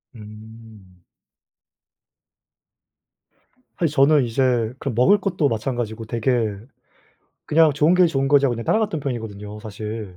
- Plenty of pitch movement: No, average, 4.8 semitones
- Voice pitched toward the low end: Yes, low, 120 Hz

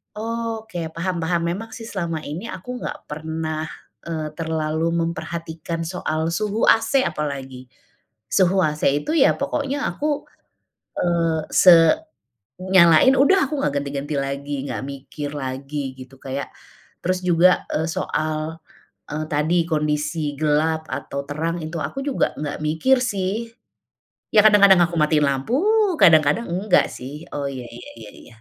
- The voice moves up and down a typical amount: Yes, average, 3.7 semitones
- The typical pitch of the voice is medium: Yes, medium, 160 Hz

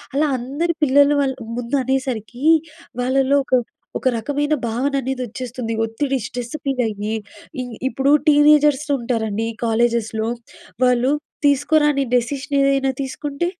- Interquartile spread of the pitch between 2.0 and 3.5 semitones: Yes, average, 3.1 semitones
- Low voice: No, very high, 265 Hz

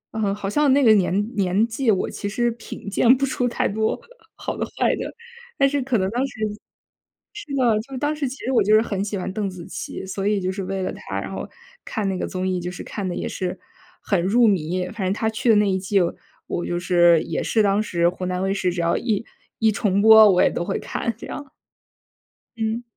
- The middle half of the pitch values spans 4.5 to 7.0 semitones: No, average, 3.9 semitones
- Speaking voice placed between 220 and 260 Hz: No, high, 205 Hz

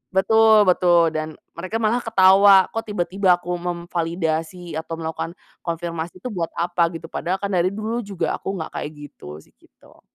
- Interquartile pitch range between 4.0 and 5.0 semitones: No, average, 3.1 semitones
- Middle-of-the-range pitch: Yes, medium, 175 Hz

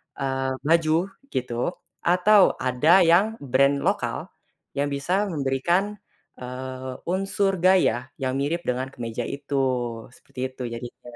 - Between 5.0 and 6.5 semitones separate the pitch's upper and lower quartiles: Yes, wide, 5.5 semitones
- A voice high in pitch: No, medium, 140 Hz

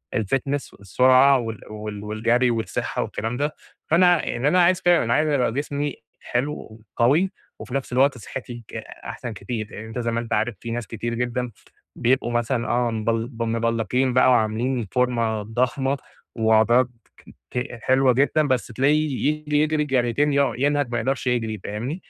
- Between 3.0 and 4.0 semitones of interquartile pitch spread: Yes, average, 3.3 semitones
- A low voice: Yes, low, 125 Hz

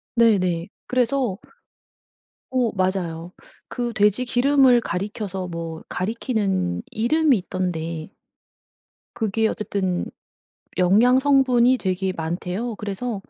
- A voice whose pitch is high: Yes, high, 205 Hz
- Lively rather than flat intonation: No, average, 5.0 semitones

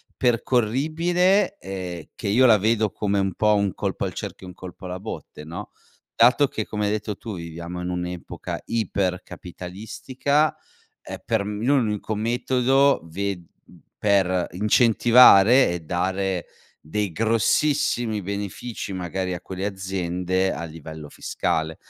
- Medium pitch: No, low, 100 Hz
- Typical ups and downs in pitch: Yes, average, 4.3 semitones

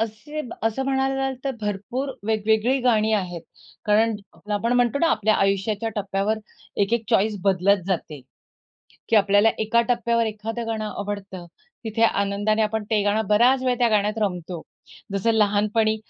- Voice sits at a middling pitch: No, high, 215 Hz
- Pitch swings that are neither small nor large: No, narrow, 2.3 semitones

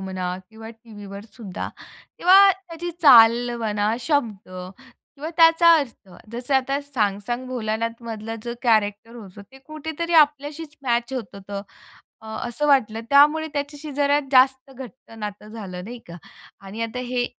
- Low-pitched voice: No, high, 240 Hz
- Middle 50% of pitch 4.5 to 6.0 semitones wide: Yes, average, 5.0 semitones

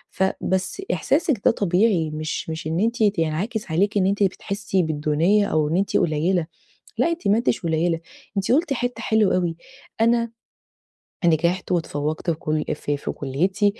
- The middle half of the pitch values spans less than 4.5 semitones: No, average, 4.9 semitones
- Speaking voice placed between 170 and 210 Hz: Yes, medium, 185 Hz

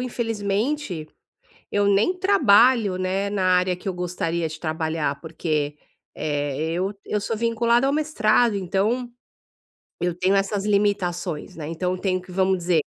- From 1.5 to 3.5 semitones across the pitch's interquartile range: No, average, 3.9 semitones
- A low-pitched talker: No, high, 190 Hz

